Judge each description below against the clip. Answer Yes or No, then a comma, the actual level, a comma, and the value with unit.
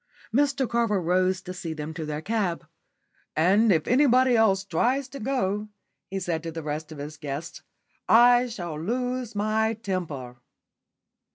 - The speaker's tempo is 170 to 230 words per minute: No, average, 155 wpm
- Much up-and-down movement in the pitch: Yes, wide, 6.5 semitones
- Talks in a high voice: Yes, high, 195 Hz